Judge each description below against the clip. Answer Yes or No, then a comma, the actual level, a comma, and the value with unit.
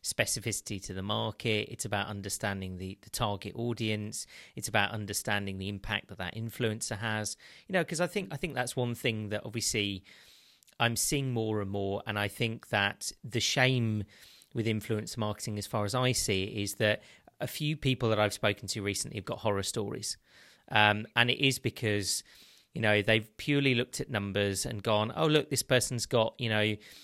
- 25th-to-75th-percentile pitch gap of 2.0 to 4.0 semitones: Yes, average, 2.9 semitones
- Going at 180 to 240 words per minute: Yes, average, 190 wpm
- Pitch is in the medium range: No, low, 110 Hz